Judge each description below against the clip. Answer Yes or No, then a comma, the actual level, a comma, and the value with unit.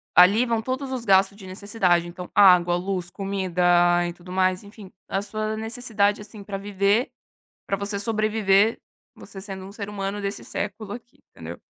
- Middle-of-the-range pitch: No, high, 200 Hz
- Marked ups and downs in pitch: No, narrow, 2.4 semitones